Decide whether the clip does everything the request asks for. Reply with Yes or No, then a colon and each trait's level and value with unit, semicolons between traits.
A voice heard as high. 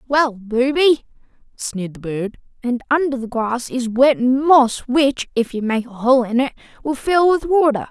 Yes: very high, 250 Hz